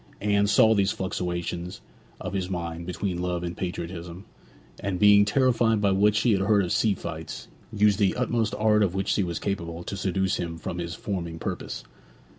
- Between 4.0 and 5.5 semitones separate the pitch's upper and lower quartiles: No, average, 3.0 semitones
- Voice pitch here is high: No, very low, 95 Hz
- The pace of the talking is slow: No, average, 185 wpm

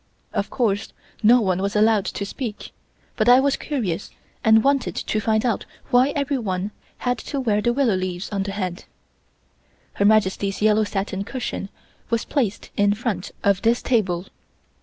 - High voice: Yes, high, 215 Hz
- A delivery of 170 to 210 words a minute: No, average, 160 wpm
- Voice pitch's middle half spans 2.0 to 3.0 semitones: No, average, 3.5 semitones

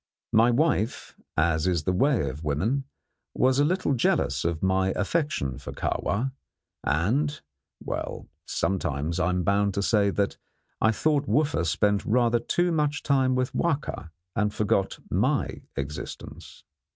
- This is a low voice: Yes, low, 105 Hz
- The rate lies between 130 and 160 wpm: Yes, average, 140 wpm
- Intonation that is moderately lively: No, wide, 7.8 semitones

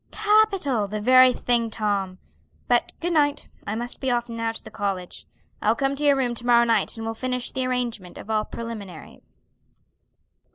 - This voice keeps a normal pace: Yes, average, 180 wpm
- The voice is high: Yes, high, 235 Hz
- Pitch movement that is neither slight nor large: Yes, average, 3.1 semitones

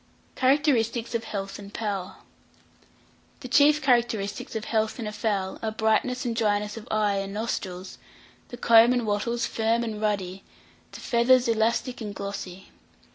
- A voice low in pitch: No, high, 220 Hz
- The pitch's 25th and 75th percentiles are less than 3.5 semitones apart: Yes, narrow, 2.5 semitones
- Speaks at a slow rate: No, average, 150 wpm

